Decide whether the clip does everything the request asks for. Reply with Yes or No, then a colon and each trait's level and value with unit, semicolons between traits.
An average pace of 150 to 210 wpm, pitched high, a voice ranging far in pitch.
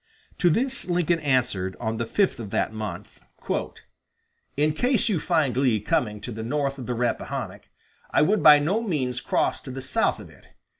No: average, 185 wpm; low, 135 Hz; wide, 6.2 semitones